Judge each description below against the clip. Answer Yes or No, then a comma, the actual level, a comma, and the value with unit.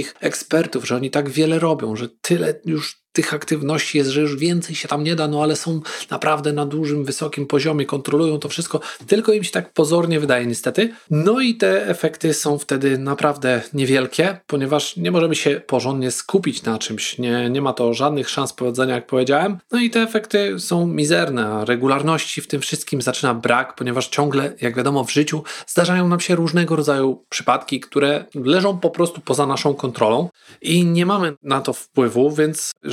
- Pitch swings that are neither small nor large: Yes, average, 3.7 semitones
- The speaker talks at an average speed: No, fast, 185 wpm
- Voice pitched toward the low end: No, medium, 150 Hz